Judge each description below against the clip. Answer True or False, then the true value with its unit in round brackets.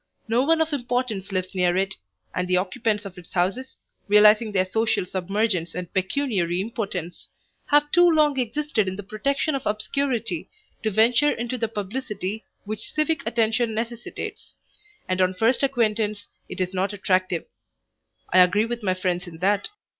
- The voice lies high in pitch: True (215 Hz)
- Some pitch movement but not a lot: True (4.6 semitones)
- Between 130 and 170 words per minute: True (160 wpm)